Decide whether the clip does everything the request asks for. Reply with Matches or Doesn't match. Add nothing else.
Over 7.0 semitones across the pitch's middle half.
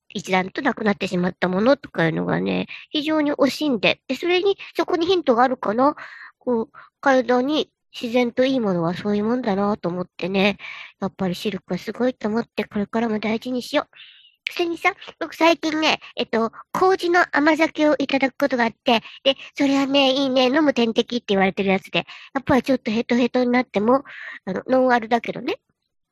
Doesn't match